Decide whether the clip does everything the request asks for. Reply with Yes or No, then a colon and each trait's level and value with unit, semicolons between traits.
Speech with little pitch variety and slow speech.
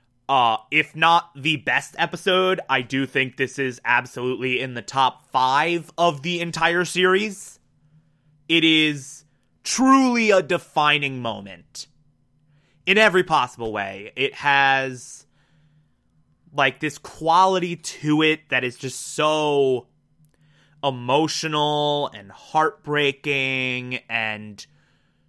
No: average, 3.7 semitones; slow, 105 wpm